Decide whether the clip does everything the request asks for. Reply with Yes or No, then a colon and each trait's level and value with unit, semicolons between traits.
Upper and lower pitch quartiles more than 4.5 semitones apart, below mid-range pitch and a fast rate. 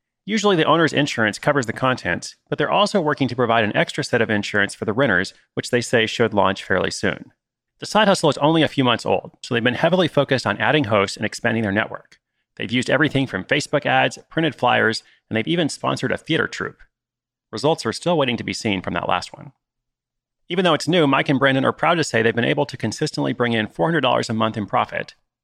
Yes: average, 4.9 semitones; low, 125 Hz; fast, 230 wpm